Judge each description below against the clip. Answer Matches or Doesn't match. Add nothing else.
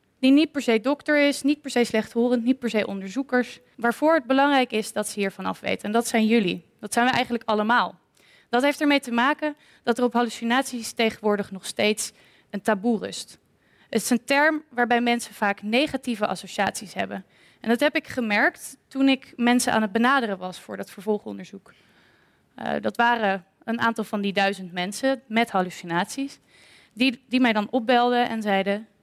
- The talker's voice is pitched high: Matches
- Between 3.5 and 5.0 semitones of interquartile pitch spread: Matches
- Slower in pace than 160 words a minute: Doesn't match